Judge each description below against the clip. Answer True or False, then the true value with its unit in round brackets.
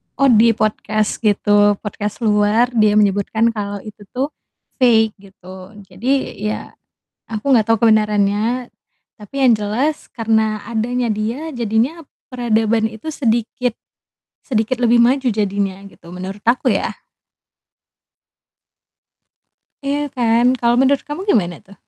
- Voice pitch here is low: False (220 Hz)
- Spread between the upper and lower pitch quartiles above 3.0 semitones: False (2.7 semitones)